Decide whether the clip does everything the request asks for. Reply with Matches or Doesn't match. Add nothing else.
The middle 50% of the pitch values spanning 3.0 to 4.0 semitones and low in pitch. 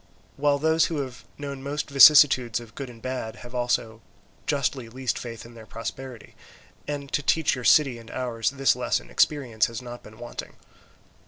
Matches